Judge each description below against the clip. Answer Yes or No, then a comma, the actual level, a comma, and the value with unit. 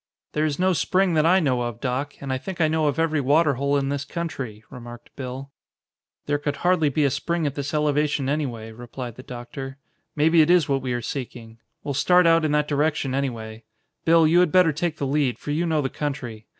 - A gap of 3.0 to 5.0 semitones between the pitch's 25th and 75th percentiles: Yes, average, 3.5 semitones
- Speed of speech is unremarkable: No, fast, 225 wpm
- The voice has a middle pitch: Yes, medium, 145 Hz